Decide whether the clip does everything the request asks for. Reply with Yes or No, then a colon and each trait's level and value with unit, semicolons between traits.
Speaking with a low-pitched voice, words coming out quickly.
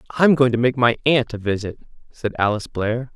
Yes: low, 120 Hz; fast, 210 wpm